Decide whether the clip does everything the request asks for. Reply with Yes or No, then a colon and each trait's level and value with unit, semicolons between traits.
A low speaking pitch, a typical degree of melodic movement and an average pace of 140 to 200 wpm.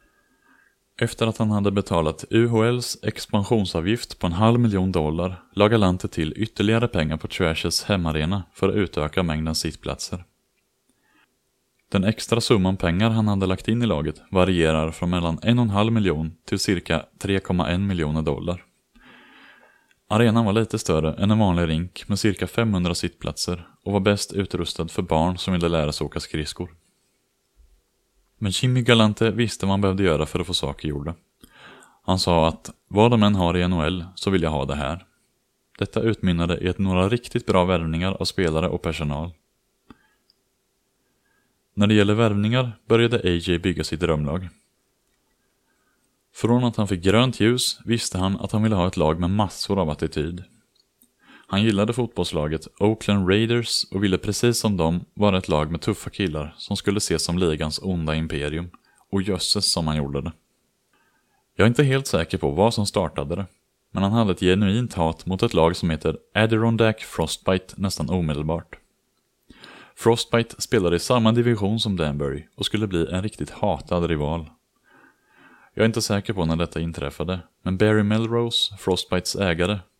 Yes: very low, 95 Hz; average, 4.4 semitones; average, 165 wpm